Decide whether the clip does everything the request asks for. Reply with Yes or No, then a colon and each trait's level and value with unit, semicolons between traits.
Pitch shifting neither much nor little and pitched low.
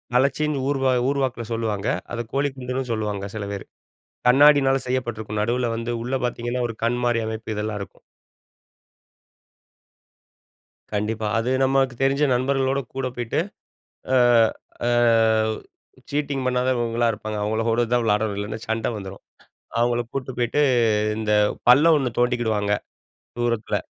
Yes: average, 3.1 semitones; low, 120 Hz